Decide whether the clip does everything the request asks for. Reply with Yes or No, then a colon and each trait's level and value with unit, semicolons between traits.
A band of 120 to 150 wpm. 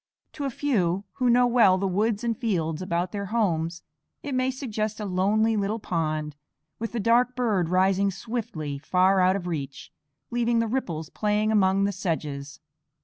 No: average, 170 wpm